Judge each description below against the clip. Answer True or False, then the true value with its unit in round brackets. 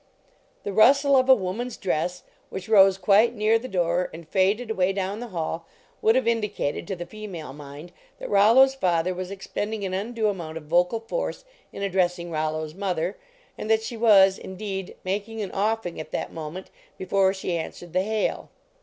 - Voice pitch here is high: True (195 Hz)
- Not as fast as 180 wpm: False (190 wpm)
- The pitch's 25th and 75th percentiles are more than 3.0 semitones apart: True (3.7 semitones)